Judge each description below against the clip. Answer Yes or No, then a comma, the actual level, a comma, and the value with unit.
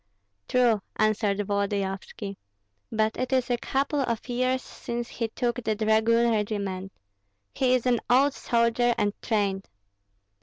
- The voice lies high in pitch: Yes, high, 230 Hz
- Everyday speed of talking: No, slow, 130 wpm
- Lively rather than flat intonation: No, average, 3.0 semitones